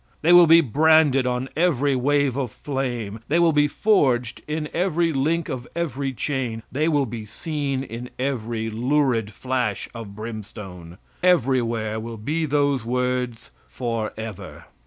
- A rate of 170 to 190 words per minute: No, average, 145 wpm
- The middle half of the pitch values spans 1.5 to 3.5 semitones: No, average, 4.4 semitones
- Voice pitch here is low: Yes, low, 130 Hz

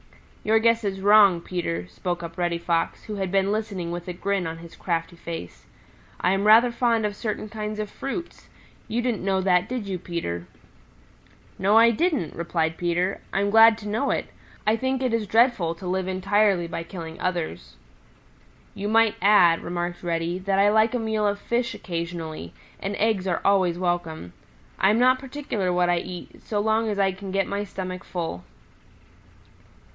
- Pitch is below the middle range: No, high, 195 Hz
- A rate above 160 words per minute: Yes, average, 180 wpm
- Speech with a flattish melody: No, average, 3.8 semitones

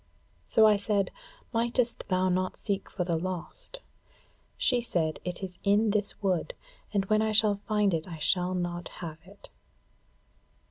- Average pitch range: Yes, average, 3.1 semitones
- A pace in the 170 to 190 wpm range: No, average, 155 wpm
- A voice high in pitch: Yes, high, 195 Hz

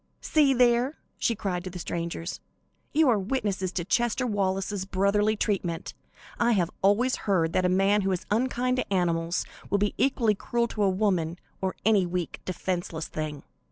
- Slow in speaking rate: No, average, 165 wpm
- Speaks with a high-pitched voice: Yes, high, 195 Hz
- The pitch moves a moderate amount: Yes, average, 4.3 semitones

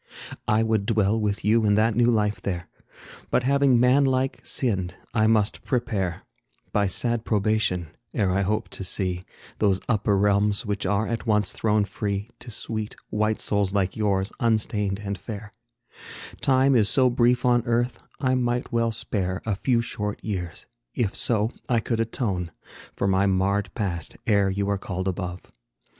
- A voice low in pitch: Yes, low, 105 Hz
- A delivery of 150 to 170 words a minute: Yes, average, 165 wpm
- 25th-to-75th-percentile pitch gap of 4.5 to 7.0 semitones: No, average, 2.9 semitones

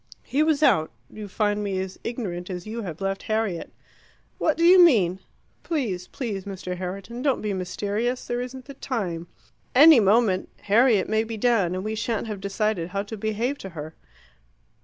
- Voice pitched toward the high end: Yes, high, 210 Hz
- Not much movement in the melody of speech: No, average, 4.3 semitones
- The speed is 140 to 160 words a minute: No, average, 180 wpm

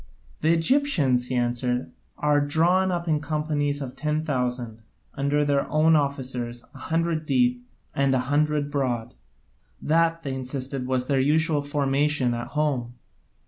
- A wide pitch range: No, average, 3.3 semitones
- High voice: No, medium, 140 Hz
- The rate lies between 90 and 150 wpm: Yes, average, 145 wpm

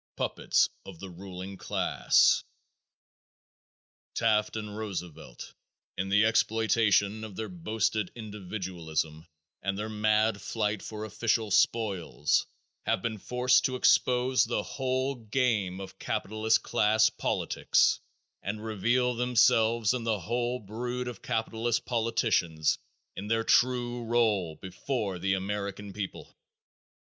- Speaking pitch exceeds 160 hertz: No, low, 110 Hz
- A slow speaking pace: Yes, slow, 115 wpm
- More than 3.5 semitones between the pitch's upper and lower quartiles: No, average, 3.2 semitones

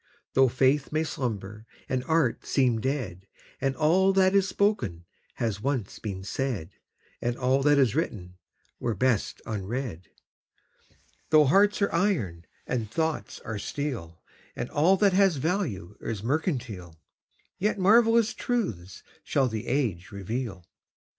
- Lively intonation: Yes, wide, 7.6 semitones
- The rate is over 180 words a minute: No, slow, 135 wpm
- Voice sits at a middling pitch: No, low, 130 Hz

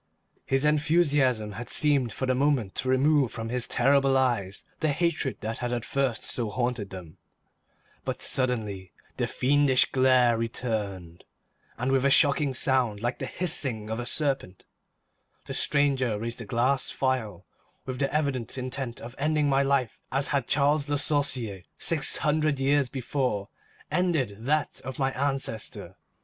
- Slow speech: No, average, 155 wpm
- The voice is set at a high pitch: No, low, 130 Hz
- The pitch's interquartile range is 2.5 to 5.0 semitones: Yes, average, 3.5 semitones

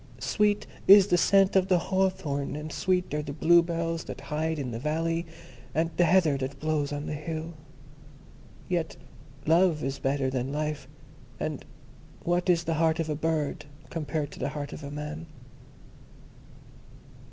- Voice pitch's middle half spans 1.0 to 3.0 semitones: Yes, average, 2.7 semitones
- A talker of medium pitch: Yes, medium, 160 Hz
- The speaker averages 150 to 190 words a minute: Yes, average, 160 wpm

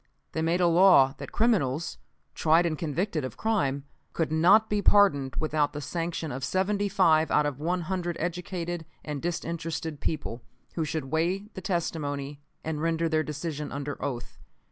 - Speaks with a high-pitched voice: No, medium, 160 Hz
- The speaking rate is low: No, average, 165 wpm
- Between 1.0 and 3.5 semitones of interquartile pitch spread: Yes, average, 3.2 semitones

